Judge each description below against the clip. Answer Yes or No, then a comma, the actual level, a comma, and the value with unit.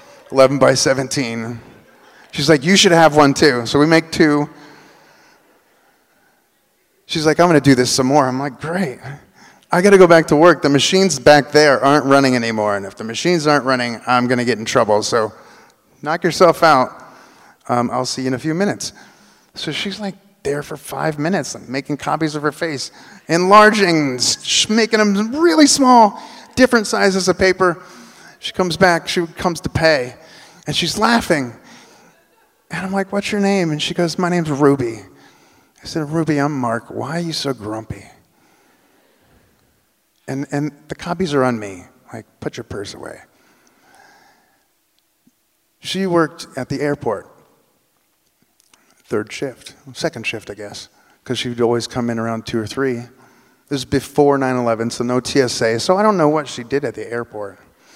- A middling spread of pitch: No, wide, 5.7 semitones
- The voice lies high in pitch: No, medium, 145 Hz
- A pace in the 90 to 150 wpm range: No, average, 175 wpm